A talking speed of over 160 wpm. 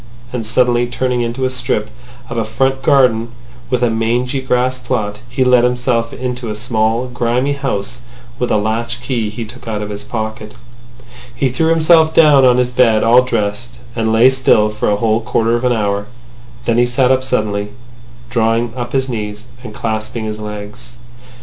Yes: average, 180 wpm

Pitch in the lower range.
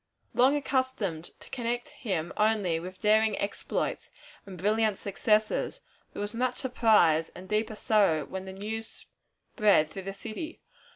No: high, 210 Hz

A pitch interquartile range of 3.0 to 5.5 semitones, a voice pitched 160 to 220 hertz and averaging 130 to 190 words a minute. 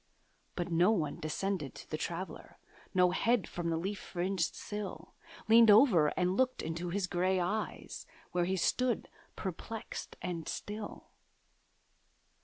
Yes: average, 3.3 semitones; medium, 185 Hz; slow, 135 wpm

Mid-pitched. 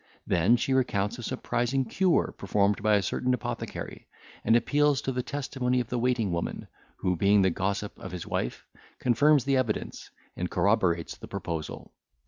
No: low, 115 Hz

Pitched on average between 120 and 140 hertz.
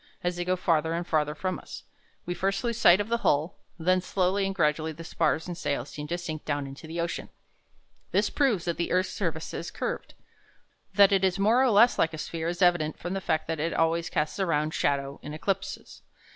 No: medium, 170 Hz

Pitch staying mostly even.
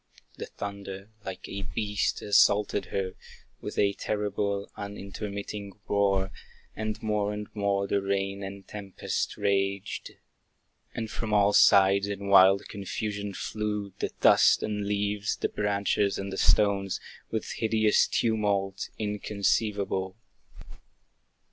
Yes: narrow, 1.1 semitones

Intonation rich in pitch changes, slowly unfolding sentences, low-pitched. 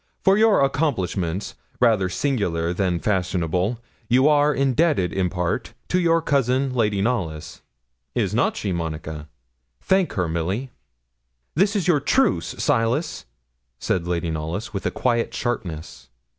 Yes: wide, 7.9 semitones; slow, 130 wpm; low, 105 Hz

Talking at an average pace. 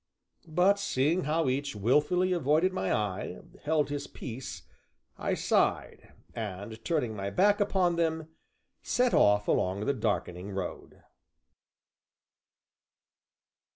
No: slow, 110 wpm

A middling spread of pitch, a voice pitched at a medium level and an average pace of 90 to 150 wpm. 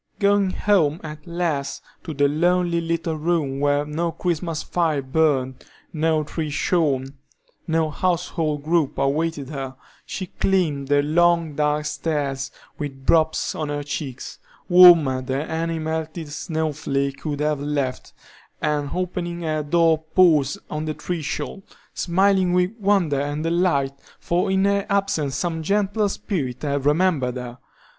Yes: average, 3.2 semitones; medium, 155 Hz; average, 140 wpm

